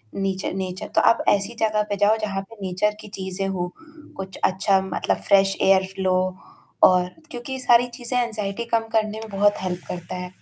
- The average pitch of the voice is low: No, high, 195 Hz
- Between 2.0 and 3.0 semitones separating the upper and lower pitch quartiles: Yes, narrow, 2.6 semitones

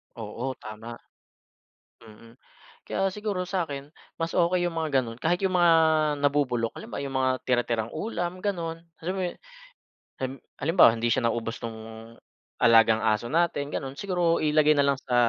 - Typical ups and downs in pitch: No, wide, 6.7 semitones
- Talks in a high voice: No, medium, 140 Hz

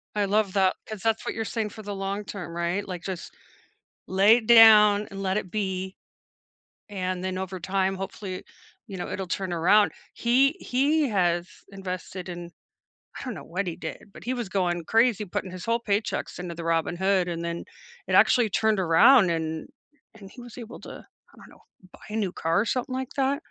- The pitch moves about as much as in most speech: Yes, average, 3.3 semitones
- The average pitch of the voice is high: Yes, high, 195 Hz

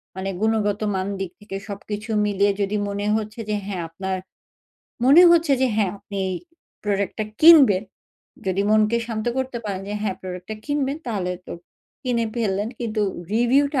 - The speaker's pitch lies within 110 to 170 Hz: No, high, 210 Hz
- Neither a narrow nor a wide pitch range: Yes, average, 3.2 semitones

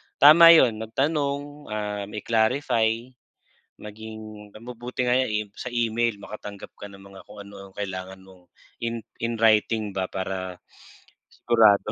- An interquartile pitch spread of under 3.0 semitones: Yes, narrow, 2.6 semitones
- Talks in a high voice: No, low, 110 Hz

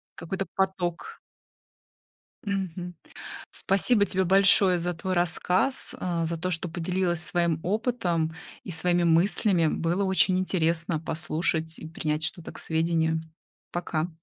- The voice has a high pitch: No, medium, 175 Hz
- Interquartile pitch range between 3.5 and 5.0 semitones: No, narrow, 2.5 semitones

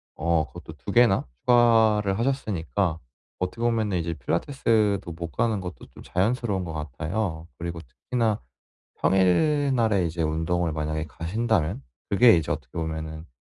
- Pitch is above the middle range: No, very low, 95 Hz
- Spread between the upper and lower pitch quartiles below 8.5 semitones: Yes, wide, 5.5 semitones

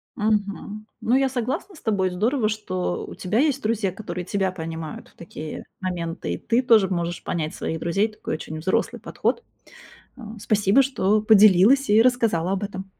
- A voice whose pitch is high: Yes, high, 205 Hz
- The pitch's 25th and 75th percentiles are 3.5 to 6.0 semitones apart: Yes, average, 4.0 semitones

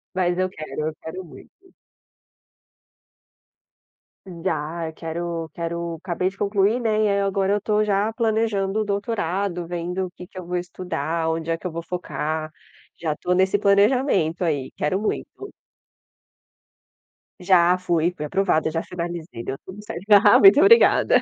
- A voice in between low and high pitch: Yes, medium, 180 Hz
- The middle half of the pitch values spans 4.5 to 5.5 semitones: No, average, 3.1 semitones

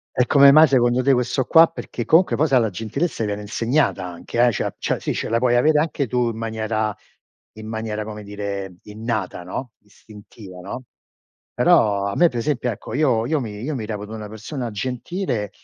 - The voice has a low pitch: Yes, low, 115 Hz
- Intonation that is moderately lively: Yes, average, 3.8 semitones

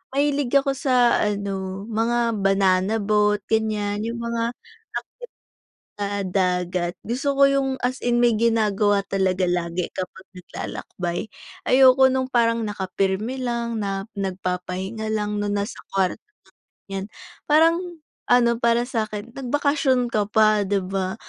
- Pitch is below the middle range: No, high, 215 Hz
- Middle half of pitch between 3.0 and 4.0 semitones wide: Yes, average, 3.7 semitones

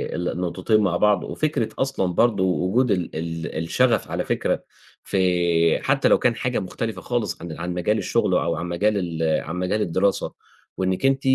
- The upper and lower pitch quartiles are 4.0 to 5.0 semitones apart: Yes, average, 4.5 semitones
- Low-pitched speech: Yes, very low, 95 Hz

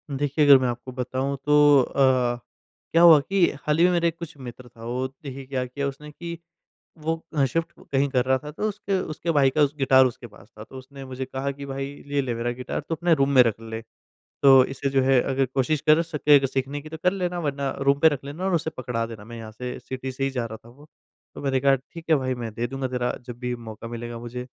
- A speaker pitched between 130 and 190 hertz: Yes, low, 135 Hz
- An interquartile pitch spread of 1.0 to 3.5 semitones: Yes, average, 2.9 semitones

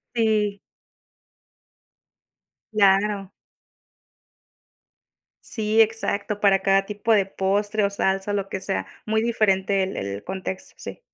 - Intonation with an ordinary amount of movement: No, narrow, 1.7 semitones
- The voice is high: Yes, high, 200 Hz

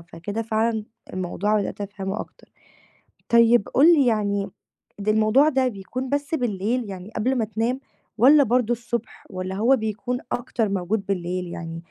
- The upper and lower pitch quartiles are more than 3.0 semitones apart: Yes, average, 3.9 semitones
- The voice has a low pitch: No, high, 220 Hz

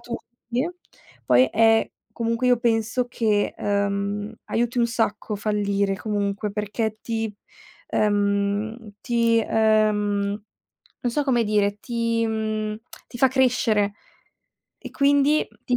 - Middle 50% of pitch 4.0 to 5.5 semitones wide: No, narrow, 2.4 semitones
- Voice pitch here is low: No, high, 220 Hz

